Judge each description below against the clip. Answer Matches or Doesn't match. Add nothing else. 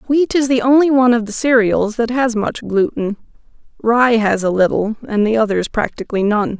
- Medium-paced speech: Matches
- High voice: Matches